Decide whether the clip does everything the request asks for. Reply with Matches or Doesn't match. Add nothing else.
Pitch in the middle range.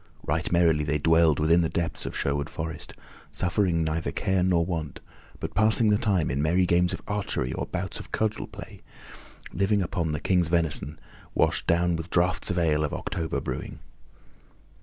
Doesn't match